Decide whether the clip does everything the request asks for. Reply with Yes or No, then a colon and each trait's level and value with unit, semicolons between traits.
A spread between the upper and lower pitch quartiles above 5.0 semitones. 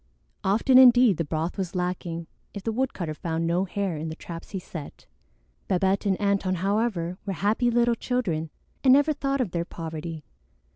Yes: wide, 5.5 semitones